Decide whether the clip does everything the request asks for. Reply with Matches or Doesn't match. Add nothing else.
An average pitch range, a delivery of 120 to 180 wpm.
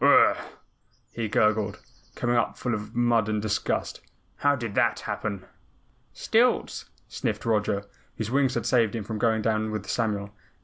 Doesn't match